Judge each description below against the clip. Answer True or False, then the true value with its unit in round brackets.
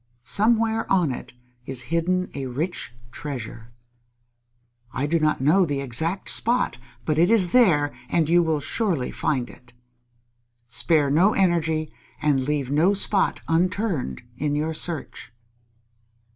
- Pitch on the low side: False (160 Hz)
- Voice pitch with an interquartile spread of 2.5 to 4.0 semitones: False (4.5 semitones)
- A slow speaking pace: True (130 wpm)